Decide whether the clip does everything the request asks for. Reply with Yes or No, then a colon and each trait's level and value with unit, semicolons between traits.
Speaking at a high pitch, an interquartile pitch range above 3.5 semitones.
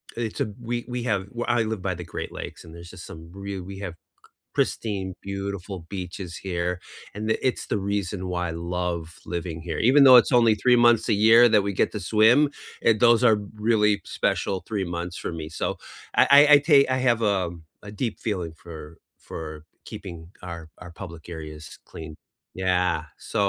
No: low, 100 Hz; average, 4.1 semitones